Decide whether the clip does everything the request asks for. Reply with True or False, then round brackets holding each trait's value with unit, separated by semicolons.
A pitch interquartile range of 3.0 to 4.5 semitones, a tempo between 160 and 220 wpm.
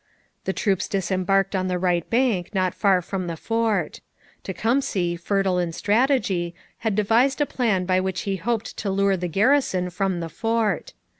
True (3.7 semitones; 165 wpm)